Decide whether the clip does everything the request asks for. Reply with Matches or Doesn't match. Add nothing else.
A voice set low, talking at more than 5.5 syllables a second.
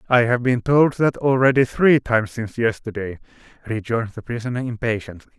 Matches